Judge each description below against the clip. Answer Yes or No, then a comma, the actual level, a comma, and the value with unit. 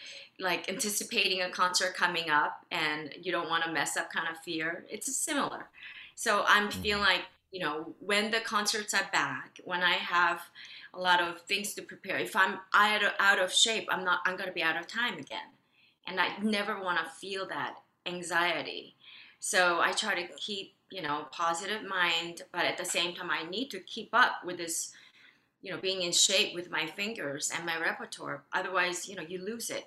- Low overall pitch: No, medium, 180 Hz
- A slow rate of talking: No, average, 200 wpm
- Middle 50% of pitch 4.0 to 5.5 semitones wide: No, average, 2.8 semitones